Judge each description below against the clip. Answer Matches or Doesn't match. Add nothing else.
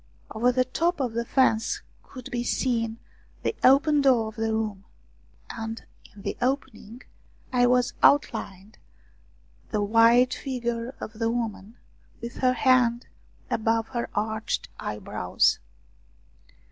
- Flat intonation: Matches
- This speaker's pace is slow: Matches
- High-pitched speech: Matches